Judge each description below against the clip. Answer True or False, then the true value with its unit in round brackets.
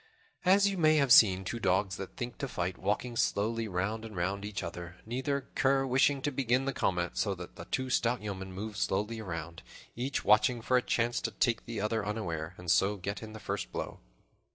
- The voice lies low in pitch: True (110 Hz)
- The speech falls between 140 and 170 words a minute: False (205 wpm)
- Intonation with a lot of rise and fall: False (4.7 semitones)